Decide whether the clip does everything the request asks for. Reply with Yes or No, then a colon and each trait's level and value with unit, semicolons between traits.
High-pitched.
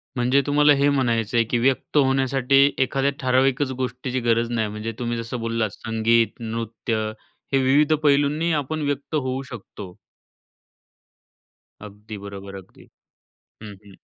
No: low, 125 Hz